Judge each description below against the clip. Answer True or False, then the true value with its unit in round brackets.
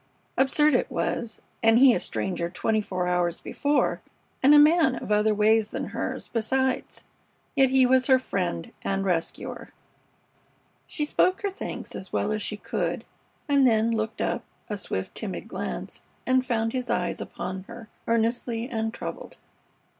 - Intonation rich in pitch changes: False (3.8 semitones)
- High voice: True (230 Hz)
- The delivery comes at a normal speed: True (155 wpm)